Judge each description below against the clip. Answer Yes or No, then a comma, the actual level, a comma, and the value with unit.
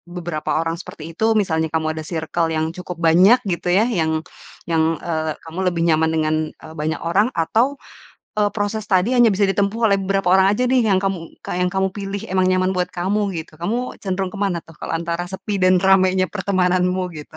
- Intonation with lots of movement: No, average, 3.1 semitones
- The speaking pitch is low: No, medium, 185 Hz